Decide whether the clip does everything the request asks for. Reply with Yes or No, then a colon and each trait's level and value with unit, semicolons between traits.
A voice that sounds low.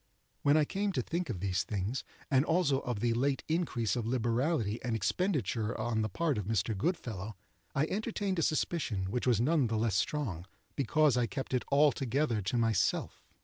Yes: low, 125 Hz